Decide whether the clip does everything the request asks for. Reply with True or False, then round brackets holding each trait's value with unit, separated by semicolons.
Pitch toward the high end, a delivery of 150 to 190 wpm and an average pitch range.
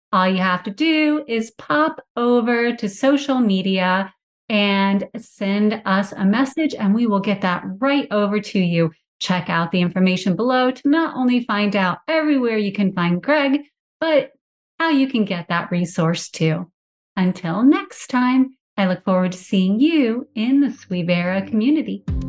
False (210 Hz; 165 wpm; 6.1 semitones)